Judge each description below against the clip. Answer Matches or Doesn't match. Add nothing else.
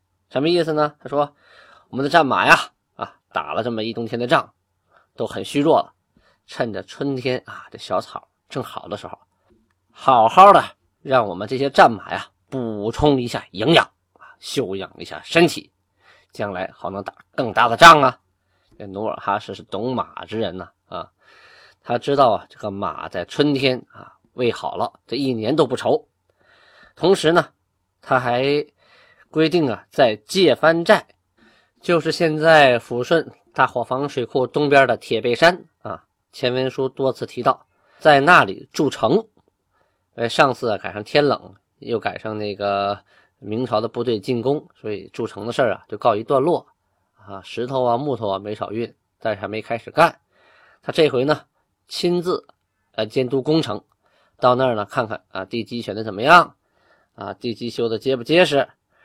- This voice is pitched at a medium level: Doesn't match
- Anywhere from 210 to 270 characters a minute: Matches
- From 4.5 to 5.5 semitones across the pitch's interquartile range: Matches